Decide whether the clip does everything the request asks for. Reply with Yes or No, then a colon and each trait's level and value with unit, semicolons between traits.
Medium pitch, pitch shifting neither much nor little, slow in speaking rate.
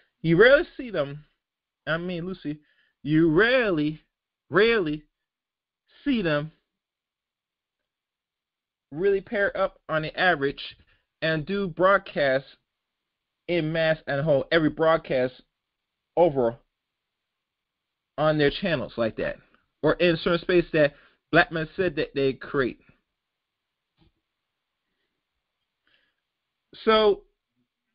Yes: medium, 160 Hz; average, 4.0 semitones; slow, 100 wpm